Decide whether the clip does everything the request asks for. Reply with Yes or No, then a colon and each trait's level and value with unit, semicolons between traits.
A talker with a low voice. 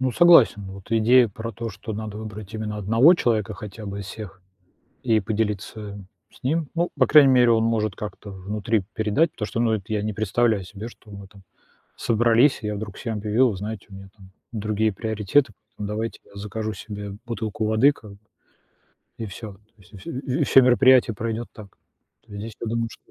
Yes: low, 110 Hz